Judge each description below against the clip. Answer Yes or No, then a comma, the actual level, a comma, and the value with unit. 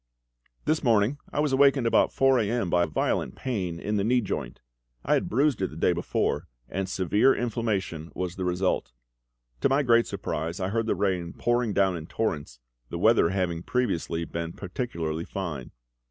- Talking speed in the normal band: Yes, average, 180 wpm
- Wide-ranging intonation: Yes, wide, 5.7 semitones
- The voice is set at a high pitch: No, very low, 95 Hz